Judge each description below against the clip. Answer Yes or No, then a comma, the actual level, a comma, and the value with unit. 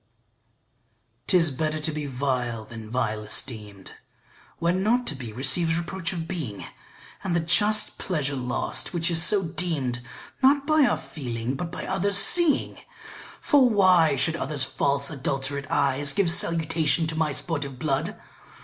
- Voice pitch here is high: No, medium, 155 Hz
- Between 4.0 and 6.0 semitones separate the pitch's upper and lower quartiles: Yes, average, 5.1 semitones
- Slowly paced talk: No, average, 150 wpm